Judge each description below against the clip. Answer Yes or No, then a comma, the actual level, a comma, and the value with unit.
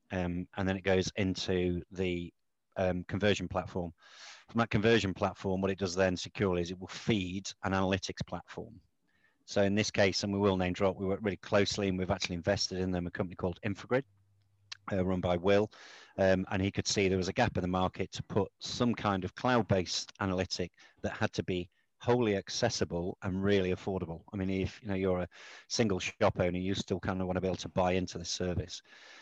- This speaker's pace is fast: Yes, fast, 215 wpm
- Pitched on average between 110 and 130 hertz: No, very low, 95 Hz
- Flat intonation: Yes, narrow, 1.8 semitones